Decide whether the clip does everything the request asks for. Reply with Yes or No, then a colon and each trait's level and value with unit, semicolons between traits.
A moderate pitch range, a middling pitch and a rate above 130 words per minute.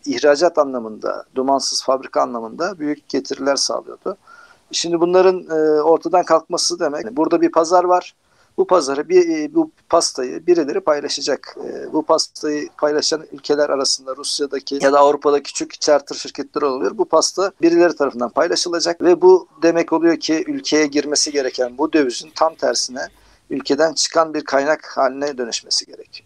Yes: average, 3.5 semitones; medium, 160 Hz; fast, 140 wpm